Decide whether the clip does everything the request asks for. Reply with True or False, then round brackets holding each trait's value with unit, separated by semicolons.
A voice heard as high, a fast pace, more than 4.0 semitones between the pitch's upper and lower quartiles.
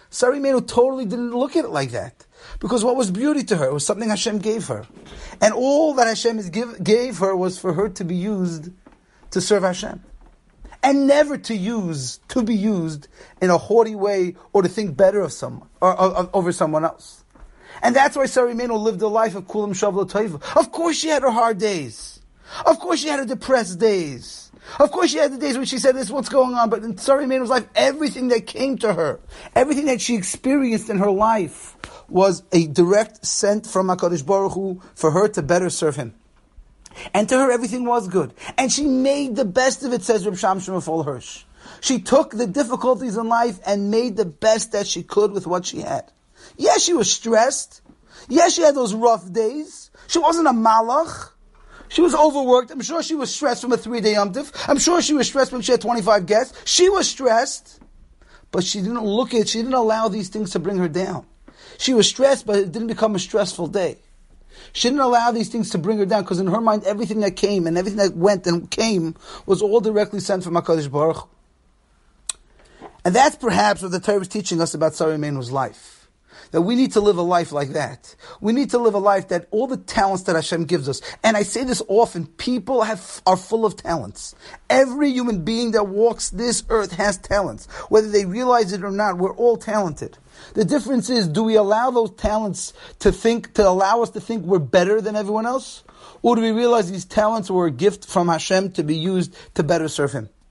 True (215 Hz; 215 wpm; 4.8 semitones)